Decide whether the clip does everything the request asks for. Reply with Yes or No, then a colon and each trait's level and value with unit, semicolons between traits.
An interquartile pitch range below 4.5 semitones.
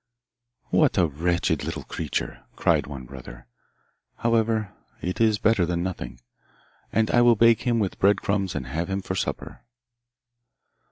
No: average, 5.1 semitones